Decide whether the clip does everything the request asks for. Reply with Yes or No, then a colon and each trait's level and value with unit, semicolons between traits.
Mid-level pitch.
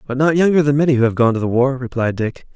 No: low, 130 Hz